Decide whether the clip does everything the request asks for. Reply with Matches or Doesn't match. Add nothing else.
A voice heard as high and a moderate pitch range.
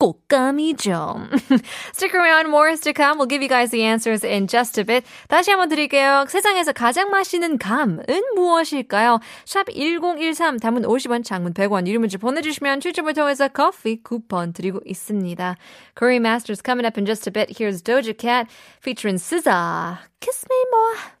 Doesn't match